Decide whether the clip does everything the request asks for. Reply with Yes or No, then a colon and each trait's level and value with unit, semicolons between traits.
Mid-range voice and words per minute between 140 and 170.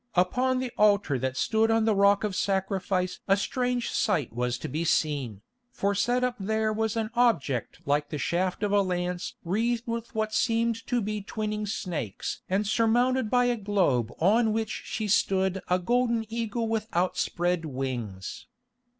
No: high, 205 Hz; average, 165 wpm